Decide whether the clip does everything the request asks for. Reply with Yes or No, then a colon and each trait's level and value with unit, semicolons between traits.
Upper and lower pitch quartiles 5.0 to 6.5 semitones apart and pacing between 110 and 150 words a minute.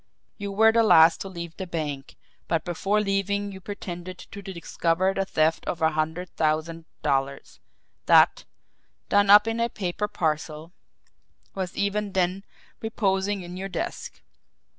No: average, 3.5 semitones; average, 145 wpm